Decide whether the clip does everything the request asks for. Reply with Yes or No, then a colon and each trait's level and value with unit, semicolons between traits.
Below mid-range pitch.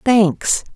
No: high, 205 Hz